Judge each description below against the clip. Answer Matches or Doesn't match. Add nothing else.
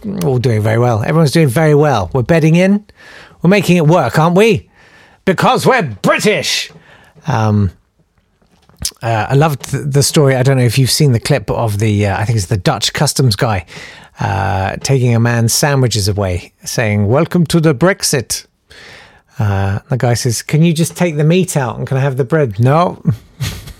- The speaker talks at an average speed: Matches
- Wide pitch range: Matches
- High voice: Doesn't match